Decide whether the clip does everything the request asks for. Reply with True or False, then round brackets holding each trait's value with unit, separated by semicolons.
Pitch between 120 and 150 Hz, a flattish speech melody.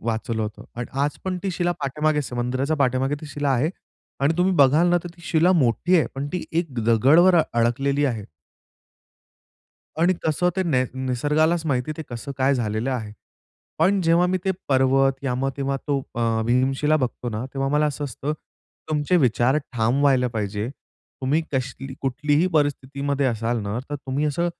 False (140 Hz; 3.9 semitones)